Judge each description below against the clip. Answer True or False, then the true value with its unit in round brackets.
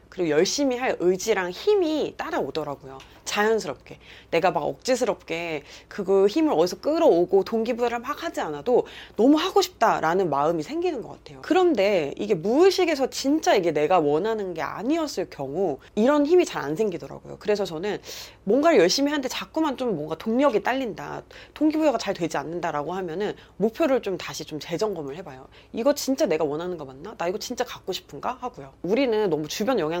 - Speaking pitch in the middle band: False (210 Hz)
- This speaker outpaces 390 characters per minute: True (400 characters per minute)